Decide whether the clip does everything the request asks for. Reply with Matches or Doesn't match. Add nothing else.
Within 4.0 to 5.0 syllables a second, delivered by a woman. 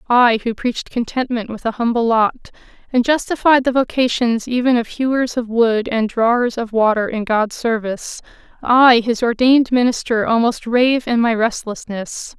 Matches